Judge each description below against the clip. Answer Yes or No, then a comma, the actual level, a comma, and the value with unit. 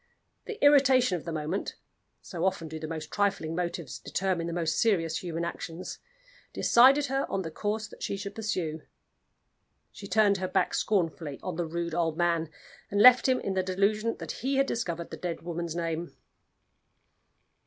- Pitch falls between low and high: Yes, medium, 180 Hz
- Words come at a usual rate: Yes, average, 175 wpm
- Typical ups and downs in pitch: Yes, average, 4.3 semitones